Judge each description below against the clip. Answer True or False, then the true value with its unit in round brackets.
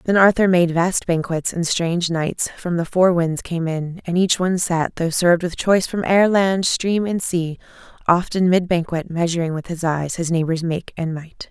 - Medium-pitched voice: True (175 Hz)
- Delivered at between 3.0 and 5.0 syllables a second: True (4.8 syllables/s)